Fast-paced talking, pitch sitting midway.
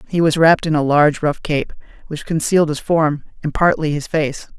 Yes: fast, 210 wpm; medium, 155 Hz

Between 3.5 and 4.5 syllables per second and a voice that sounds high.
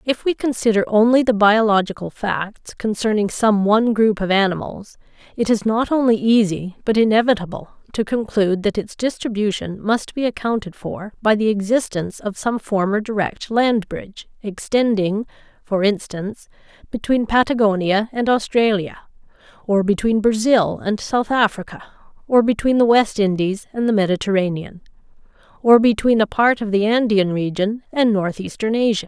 No: 5.0 syllables/s; high, 215 Hz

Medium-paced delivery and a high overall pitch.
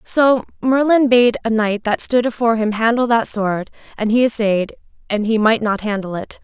Yes: average, 195 wpm; high, 225 Hz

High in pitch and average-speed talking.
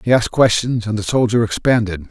No: low, 110 Hz; average, 170 wpm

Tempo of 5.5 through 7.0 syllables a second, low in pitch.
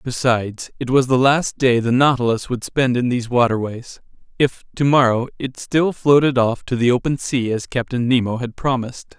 No: 5.2 syllables/s; low, 125 Hz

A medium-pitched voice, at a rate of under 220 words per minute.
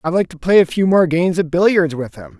No: medium, 170 Hz; fast, 300 wpm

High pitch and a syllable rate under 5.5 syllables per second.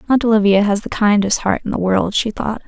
No: high, 210 Hz; 5.8 syllables/s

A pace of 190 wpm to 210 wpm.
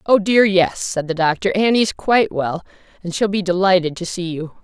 Yes: fast, 205 wpm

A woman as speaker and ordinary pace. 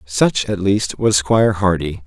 No: male; average, 175 wpm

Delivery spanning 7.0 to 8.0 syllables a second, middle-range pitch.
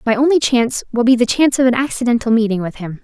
No: 7.1 syllables/s; high, 240 Hz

